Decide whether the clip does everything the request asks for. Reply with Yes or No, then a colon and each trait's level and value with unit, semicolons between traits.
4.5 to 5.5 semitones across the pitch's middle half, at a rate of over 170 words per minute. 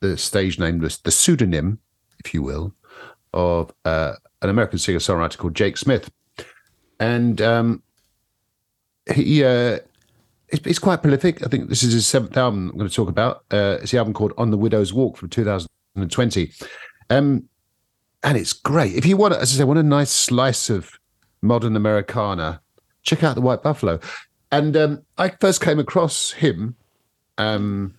No: average, 5.1 semitones; average, 165 wpm